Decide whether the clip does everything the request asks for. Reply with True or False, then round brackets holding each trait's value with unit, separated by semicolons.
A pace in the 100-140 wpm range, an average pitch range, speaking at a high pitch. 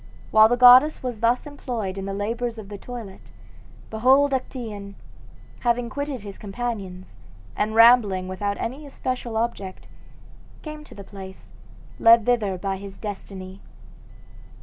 True (135 wpm; 3.8 semitones; 220 Hz)